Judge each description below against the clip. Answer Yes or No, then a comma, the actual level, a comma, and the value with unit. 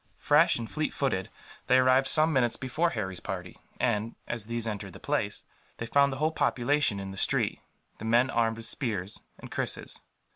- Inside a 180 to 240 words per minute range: Yes, average, 185 wpm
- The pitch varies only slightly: No, average, 4.0 semitones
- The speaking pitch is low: Yes, low, 120 Hz